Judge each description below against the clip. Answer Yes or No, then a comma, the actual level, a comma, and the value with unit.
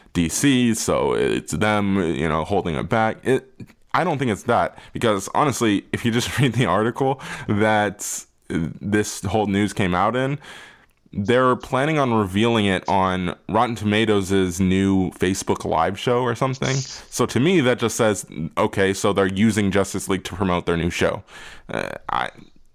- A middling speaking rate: Yes, average, 165 wpm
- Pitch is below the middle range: Yes, low, 105 Hz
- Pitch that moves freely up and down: No, average, 3.8 semitones